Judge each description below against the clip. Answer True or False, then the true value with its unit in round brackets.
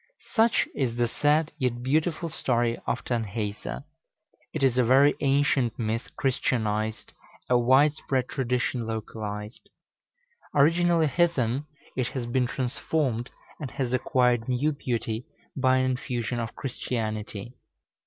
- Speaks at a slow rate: True (125 wpm)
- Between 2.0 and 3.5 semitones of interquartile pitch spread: True (3.1 semitones)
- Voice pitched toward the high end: False (125 Hz)